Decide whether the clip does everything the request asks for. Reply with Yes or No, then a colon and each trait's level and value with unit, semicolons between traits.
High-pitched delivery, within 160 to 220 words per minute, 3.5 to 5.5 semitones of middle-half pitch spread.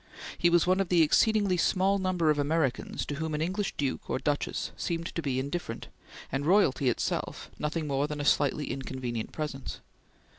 No: medium, 155 Hz; average, 180 wpm; average, 4.0 semitones